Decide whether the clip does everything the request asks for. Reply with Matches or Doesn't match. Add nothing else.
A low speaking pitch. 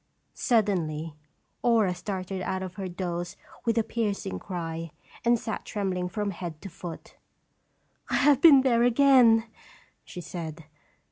Doesn't match